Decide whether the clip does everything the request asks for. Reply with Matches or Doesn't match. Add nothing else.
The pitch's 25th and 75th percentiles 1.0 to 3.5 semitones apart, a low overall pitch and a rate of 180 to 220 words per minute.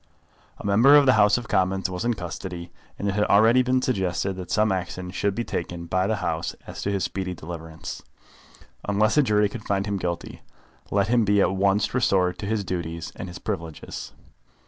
Matches